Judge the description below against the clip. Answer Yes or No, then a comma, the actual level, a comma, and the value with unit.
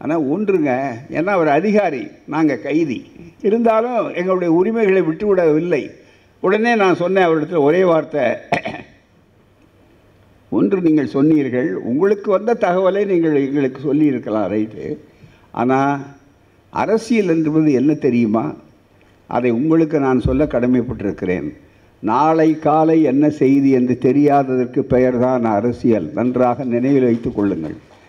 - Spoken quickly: No, average, 105 wpm